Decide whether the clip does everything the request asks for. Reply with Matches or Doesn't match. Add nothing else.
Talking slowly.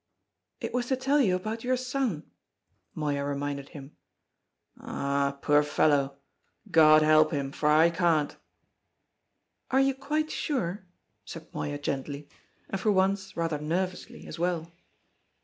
Matches